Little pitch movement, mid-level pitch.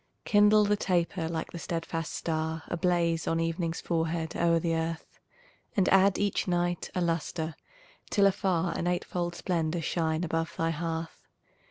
Yes: narrow, 1.5 semitones; medium, 170 Hz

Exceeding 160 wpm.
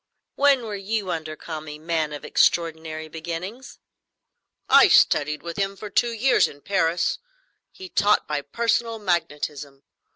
No: slow, 135 wpm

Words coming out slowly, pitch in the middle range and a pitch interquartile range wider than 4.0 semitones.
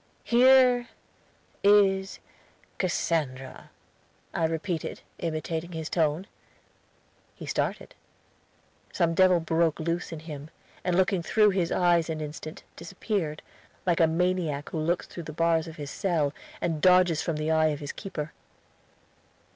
No: slow, 130 wpm; medium, 165 Hz; average, 2.7 semitones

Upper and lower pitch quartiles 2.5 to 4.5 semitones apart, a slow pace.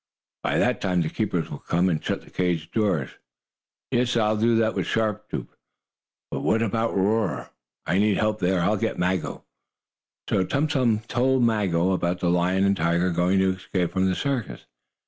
No: average, 3.9 semitones; average, 185 wpm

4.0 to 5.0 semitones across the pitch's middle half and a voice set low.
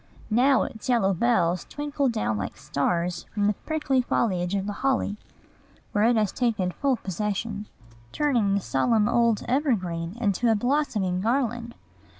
No: average, 4.6 semitones; high, 215 Hz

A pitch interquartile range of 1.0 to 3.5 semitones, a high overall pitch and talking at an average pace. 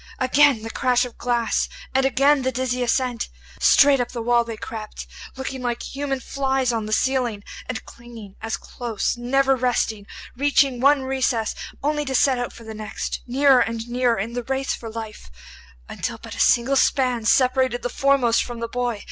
Yes: narrow, 2.4 semitones; high, 245 Hz; average, 180 wpm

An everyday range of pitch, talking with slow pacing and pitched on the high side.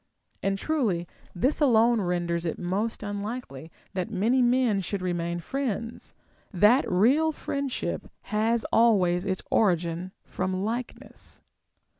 Yes: average, 5.0 semitones; slow, 120 wpm; high, 205 Hz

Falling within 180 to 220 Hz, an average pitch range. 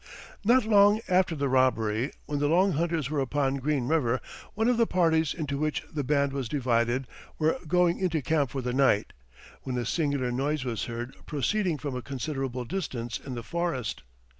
No: medium, 140 Hz; average, 4.5 semitones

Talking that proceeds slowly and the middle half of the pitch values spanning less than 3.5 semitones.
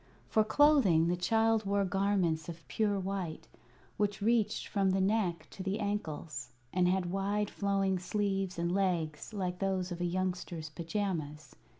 No: average, 155 wpm; average, 2.7 semitones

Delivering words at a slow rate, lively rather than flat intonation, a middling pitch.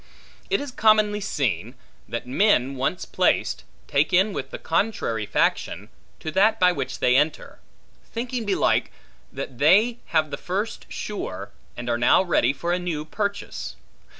No: average, 150 wpm; wide, 7.4 semitones; medium, 180 Hz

